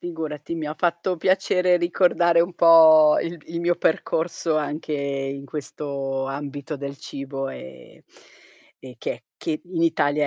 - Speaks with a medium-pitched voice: Yes, medium, 155 Hz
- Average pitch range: Yes, average, 3.4 semitones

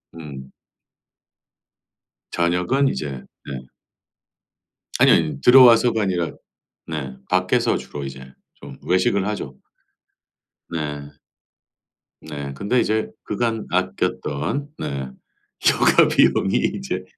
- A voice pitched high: No, very low, 80 Hz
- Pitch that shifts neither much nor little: No, wide, 7.3 semitones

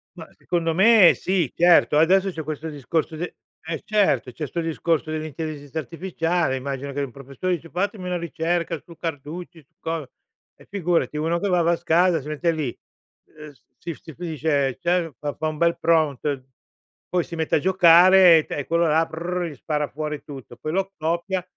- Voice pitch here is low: No, medium, 165 Hz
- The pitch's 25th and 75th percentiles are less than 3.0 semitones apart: Yes, narrow, 2.6 semitones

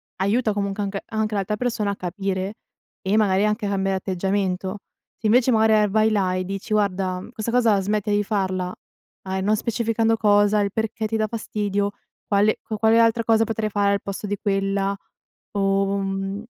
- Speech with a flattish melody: Yes, narrow, 1.9 semitones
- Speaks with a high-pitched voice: Yes, high, 205 Hz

